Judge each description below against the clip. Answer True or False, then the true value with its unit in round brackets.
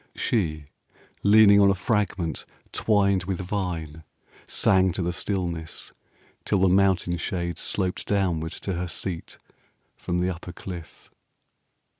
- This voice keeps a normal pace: False (130 wpm)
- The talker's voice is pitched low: True (90 Hz)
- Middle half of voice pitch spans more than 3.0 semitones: False (2.4 semitones)